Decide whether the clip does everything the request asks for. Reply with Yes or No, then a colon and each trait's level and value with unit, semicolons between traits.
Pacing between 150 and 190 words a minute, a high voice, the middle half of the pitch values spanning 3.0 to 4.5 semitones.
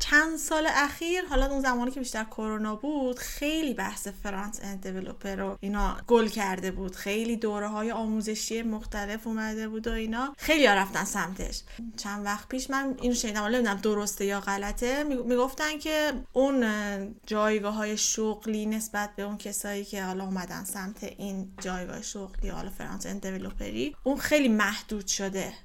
Yes: fast, 155 wpm; high, 215 Hz; average, 3.7 semitones